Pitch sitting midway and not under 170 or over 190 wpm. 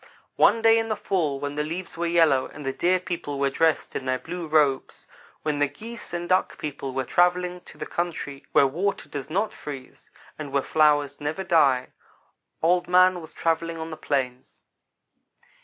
Yes: medium, 160 Hz; average, 185 wpm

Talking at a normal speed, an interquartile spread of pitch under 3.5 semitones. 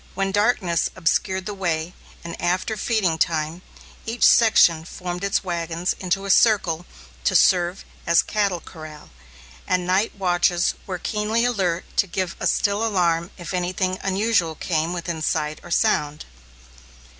Yes: average, 145 wpm; average, 2.7 semitones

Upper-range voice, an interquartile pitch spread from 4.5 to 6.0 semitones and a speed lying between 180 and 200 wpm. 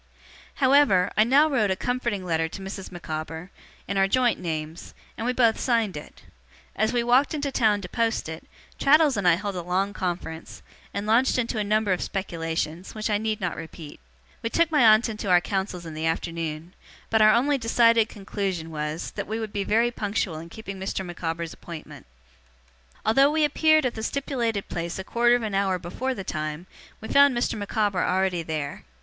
Yes: high, 205 Hz; average, 5.3 semitones; average, 195 wpm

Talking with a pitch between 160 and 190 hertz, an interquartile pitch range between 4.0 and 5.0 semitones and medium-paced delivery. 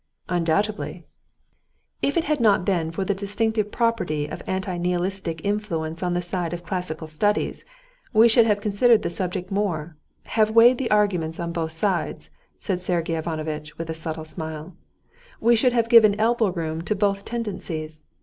Yes: medium, 185 Hz; average, 4.6 semitones; average, 165 wpm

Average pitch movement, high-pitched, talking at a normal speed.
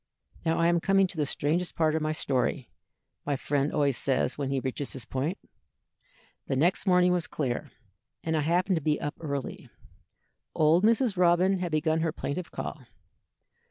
No: average, 3.7 semitones; medium, 160 Hz; average, 175 wpm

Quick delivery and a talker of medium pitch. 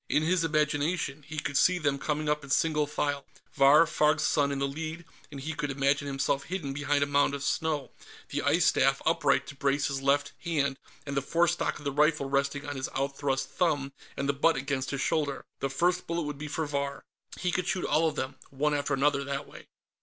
Yes: fast, 220 wpm; medium, 145 Hz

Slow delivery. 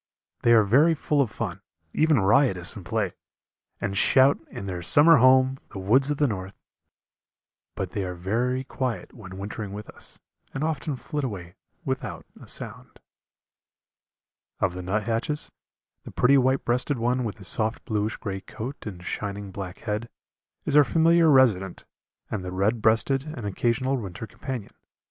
No: average, 160 wpm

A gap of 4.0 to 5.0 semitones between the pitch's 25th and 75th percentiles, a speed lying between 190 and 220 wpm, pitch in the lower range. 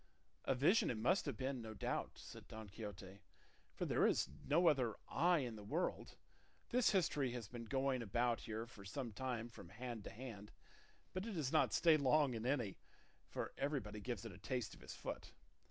Yes: average, 4.3 semitones; average, 195 wpm; low, 125 Hz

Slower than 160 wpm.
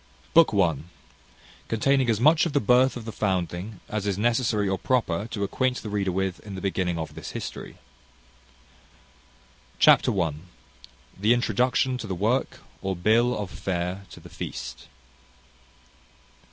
Yes: average, 150 wpm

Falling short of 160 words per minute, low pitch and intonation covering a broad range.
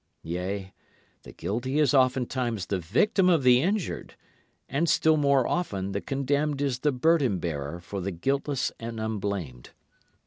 Yes: average, 145 wpm; low, 125 Hz; wide, 6.5 semitones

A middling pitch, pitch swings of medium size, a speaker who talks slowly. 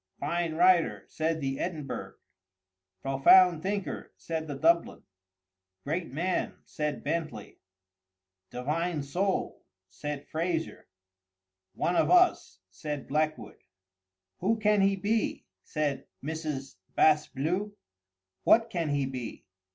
Yes: medium, 160 Hz; average, 3.9 semitones; slow, 105 wpm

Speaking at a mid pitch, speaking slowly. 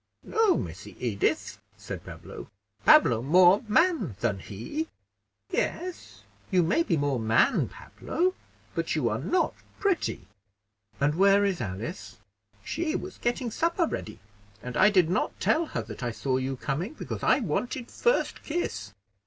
No: medium, 180 Hz; average, 150 wpm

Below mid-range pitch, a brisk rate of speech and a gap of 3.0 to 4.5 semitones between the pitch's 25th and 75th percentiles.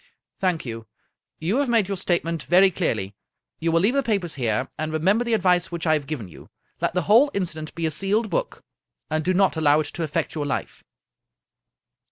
No: medium, 170 Hz; fast, 215 wpm; average, 4.0 semitones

